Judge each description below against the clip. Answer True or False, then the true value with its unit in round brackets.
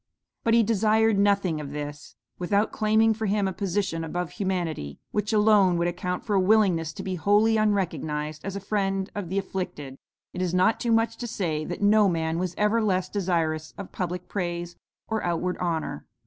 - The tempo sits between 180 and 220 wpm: True (190 wpm)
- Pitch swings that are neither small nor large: True (3.5 semitones)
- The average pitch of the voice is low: False (190 Hz)